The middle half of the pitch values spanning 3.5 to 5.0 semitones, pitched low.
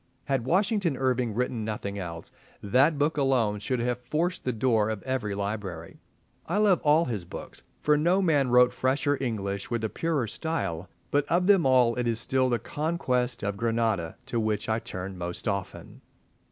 No: wide, 5.4 semitones; low, 125 Hz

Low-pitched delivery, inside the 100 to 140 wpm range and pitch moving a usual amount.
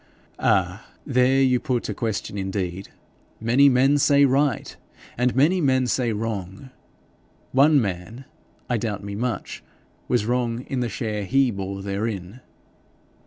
Yes: low, 120 Hz; slow, 135 wpm; average, 4.5 semitones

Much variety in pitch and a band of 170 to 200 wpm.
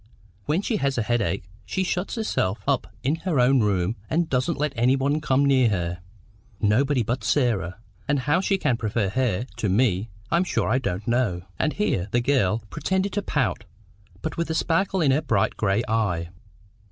Yes: wide, 6.5 semitones; average, 185 wpm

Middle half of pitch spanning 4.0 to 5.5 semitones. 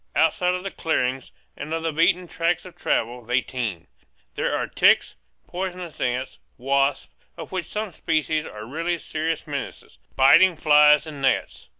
Yes: average, 4.4 semitones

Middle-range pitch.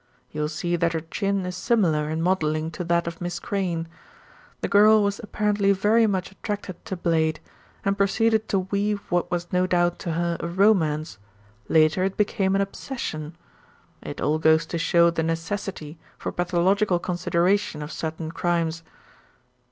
Yes: medium, 175 Hz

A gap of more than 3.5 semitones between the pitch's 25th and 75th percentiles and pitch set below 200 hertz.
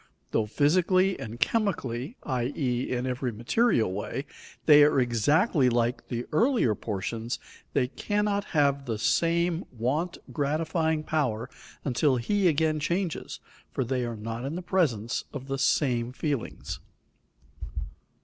Yes: wide, 5.4 semitones; medium, 140 Hz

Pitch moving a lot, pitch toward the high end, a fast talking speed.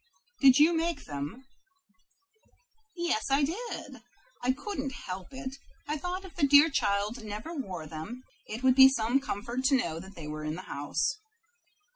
No: wide, 6.5 semitones; very high, 260 Hz; average, 160 wpm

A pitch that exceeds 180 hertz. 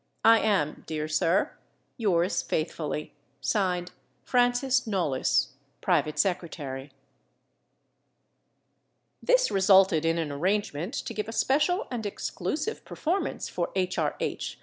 Yes: high, 190 Hz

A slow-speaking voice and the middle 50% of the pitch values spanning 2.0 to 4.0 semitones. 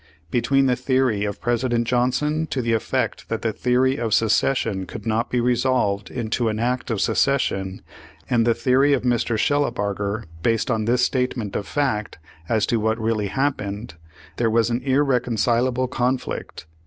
No: average, 165 wpm; average, 2.7 semitones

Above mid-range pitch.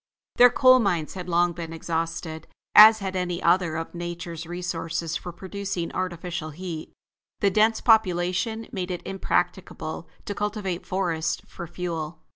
No: medium, 175 Hz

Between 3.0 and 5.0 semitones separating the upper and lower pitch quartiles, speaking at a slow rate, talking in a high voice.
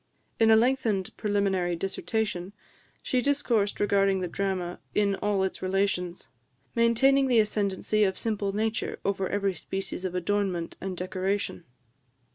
No: narrow, 2.6 semitones; slow, 130 wpm; high, 200 Hz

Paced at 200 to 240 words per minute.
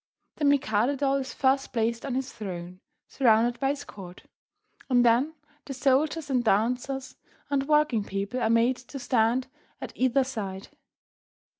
No: average, 150 wpm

